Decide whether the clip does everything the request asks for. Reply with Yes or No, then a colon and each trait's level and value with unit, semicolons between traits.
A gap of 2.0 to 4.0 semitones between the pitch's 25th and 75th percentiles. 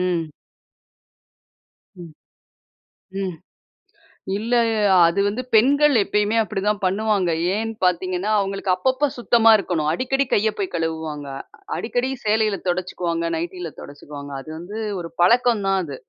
No: average, 4.7 semitones